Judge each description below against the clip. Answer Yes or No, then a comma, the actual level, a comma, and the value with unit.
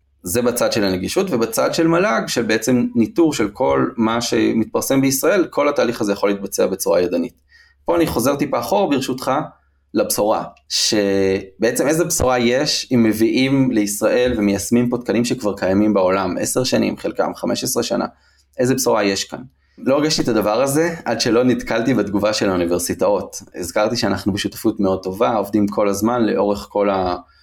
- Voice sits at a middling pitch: No, low, 110 Hz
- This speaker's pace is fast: Yes, fast, 160 wpm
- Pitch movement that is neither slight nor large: Yes, average, 3.9 semitones